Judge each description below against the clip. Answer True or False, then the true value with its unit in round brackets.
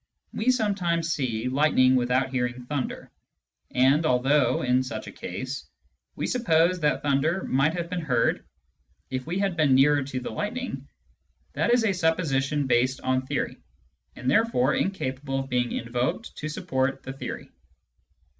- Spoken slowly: False (150 wpm)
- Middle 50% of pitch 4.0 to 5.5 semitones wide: True (4.5 semitones)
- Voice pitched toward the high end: False (135 Hz)